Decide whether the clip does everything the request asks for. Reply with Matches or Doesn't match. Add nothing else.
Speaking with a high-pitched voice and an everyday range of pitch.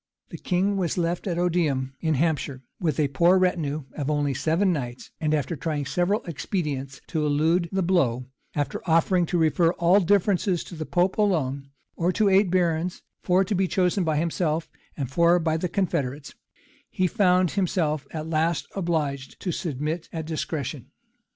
Doesn't match